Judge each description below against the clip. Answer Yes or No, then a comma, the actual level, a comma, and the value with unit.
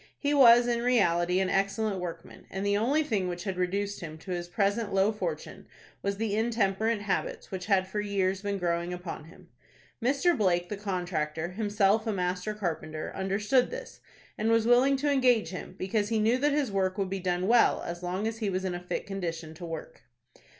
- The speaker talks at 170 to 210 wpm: Yes, average, 200 wpm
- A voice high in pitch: Yes, high, 195 Hz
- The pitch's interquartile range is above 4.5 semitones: No, average, 3.7 semitones